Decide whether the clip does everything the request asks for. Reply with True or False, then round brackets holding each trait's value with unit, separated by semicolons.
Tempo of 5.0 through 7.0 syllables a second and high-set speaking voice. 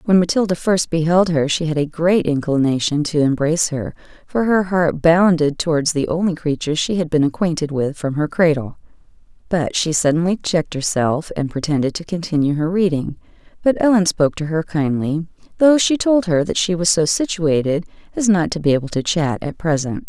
False (5.4 syllables/s; 165 Hz)